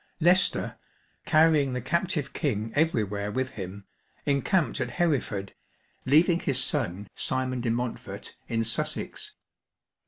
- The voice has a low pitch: Yes, low, 130 Hz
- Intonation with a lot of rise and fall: Yes, wide, 5.7 semitones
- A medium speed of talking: No, slow, 115 wpm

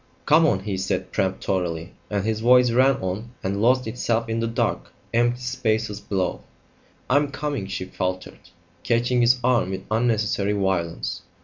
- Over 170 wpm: No, average, 150 wpm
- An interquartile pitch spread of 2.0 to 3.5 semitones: No, average, 4.3 semitones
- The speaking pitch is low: Yes, low, 110 Hz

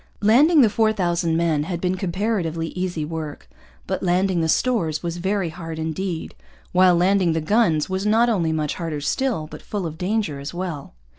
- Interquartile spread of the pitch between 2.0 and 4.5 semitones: Yes, average, 3.7 semitones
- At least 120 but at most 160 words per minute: No, average, 180 wpm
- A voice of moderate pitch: Yes, medium, 175 Hz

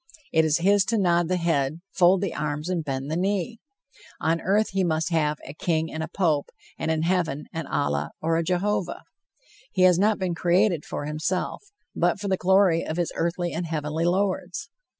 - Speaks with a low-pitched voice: No, medium, 170 Hz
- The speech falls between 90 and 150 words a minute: No, average, 195 wpm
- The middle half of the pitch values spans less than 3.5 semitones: Yes, average, 2.8 semitones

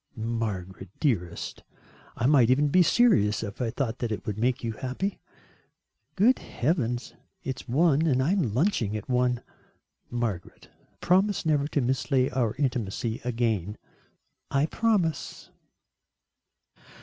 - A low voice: Yes, low, 125 Hz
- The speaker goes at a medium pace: No, slow, 125 wpm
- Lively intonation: No, average, 5.0 semitones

